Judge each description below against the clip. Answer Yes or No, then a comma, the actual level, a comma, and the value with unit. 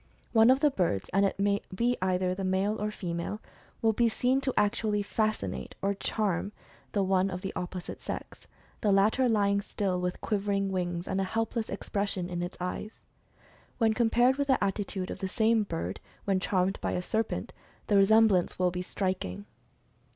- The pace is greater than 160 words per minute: Yes, average, 180 wpm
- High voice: Yes, high, 200 Hz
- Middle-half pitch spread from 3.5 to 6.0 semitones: No, average, 3.0 semitones